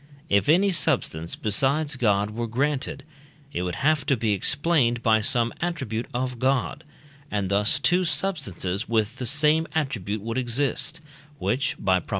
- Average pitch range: No, wide, 5.7 semitones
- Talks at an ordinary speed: Yes, average, 155 wpm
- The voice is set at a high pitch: No, low, 125 Hz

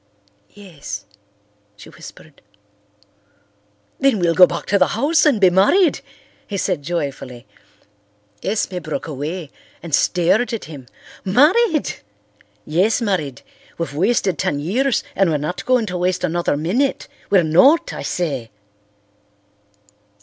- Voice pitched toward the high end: No, medium, 180 Hz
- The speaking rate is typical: No, slow, 125 wpm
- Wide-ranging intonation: Yes, wide, 6.1 semitones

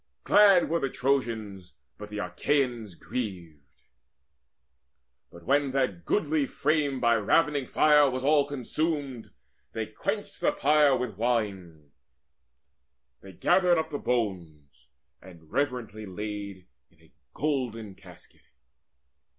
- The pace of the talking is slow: Yes, slow, 115 wpm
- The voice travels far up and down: Yes, wide, 6.7 semitones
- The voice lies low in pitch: Yes, low, 125 Hz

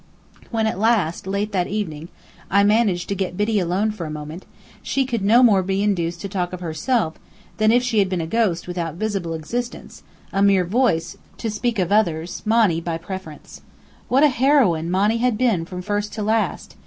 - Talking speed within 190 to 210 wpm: Yes, average, 195 wpm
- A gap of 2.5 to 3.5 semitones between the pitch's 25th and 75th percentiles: No, average, 4.2 semitones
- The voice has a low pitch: No, high, 200 Hz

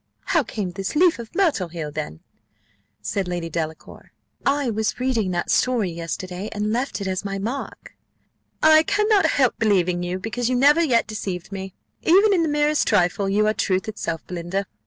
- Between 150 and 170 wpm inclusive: No, average, 180 wpm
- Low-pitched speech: No, high, 210 Hz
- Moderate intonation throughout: No, wide, 7.1 semitones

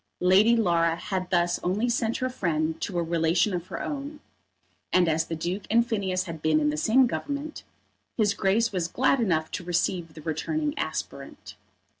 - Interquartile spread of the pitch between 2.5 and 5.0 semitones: No, wide, 5.6 semitones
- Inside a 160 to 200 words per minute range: Yes, average, 180 wpm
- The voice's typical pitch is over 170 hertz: Yes, medium, 185 Hz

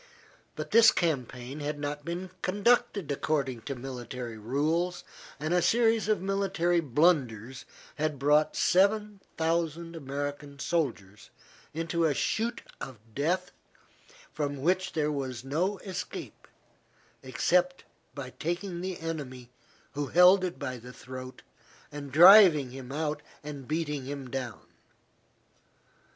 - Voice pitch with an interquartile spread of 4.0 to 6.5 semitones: Yes, average, 4.9 semitones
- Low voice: No, medium, 155 Hz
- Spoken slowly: Yes, slow, 120 wpm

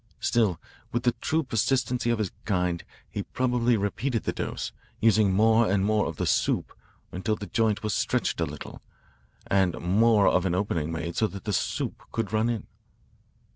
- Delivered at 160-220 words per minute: Yes, average, 175 wpm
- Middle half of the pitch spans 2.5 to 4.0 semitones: Yes, average, 3.5 semitones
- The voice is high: No, low, 105 Hz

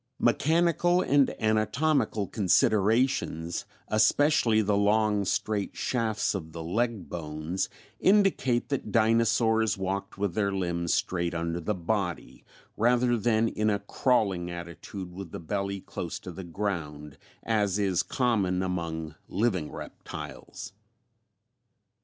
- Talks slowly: Yes, slow, 115 wpm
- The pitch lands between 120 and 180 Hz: No, low, 100 Hz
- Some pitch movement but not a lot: Yes, average, 4.5 semitones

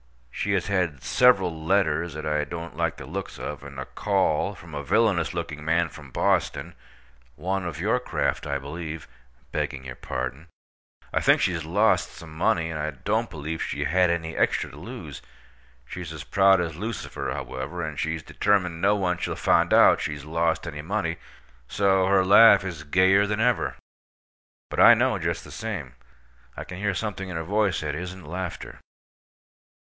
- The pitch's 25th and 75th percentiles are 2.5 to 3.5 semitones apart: No, average, 3.9 semitones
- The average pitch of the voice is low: Yes, very low, 85 Hz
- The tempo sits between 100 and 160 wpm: No, average, 175 wpm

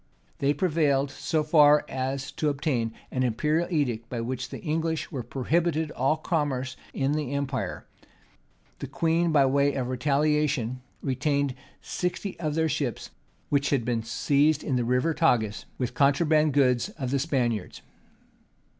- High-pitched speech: No, medium, 140 Hz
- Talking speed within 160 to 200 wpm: No, average, 145 wpm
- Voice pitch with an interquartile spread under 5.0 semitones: Yes, average, 3.2 semitones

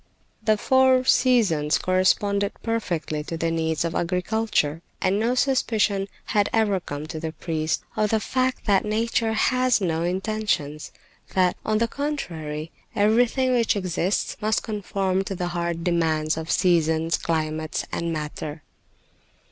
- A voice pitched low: No, medium, 185 Hz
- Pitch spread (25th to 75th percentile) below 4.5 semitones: No, average, 5.2 semitones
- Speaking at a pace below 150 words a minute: Yes, average, 140 wpm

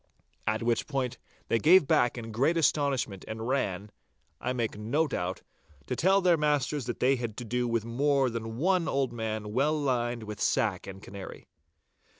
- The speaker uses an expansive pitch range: No, average, 4.2 semitones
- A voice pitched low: Yes, low, 120 Hz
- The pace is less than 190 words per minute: Yes, average, 170 wpm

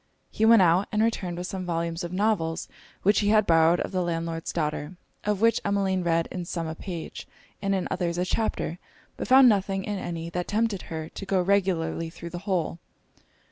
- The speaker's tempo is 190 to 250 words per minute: Yes, average, 200 wpm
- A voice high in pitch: No, medium, 180 Hz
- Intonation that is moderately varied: Yes, average, 3.1 semitones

